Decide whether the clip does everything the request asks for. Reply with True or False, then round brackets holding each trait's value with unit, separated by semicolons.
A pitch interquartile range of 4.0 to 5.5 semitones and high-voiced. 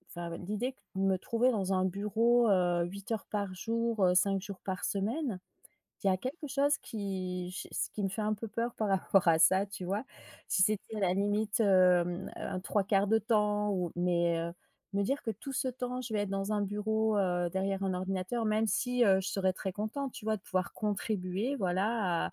False (2.9 semitones; 200 Hz)